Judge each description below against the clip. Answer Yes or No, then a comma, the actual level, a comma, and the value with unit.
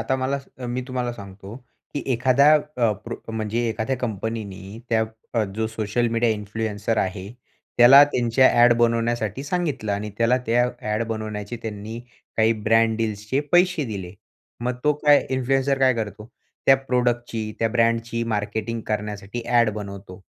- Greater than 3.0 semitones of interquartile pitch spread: No, average, 2.7 semitones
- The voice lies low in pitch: Yes, low, 115 Hz